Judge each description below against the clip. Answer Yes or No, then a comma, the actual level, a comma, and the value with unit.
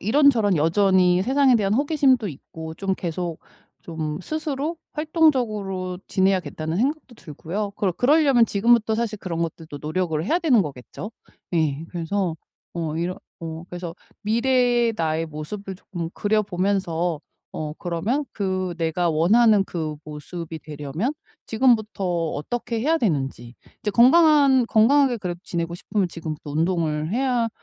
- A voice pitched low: No, high, 190 Hz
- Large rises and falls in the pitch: Yes, wide, 6.4 semitones